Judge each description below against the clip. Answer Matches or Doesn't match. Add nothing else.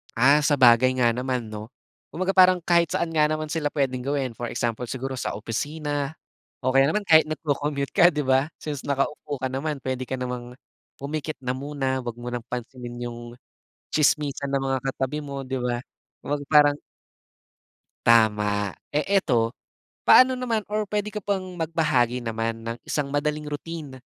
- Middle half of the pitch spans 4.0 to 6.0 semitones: Doesn't match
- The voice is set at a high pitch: Doesn't match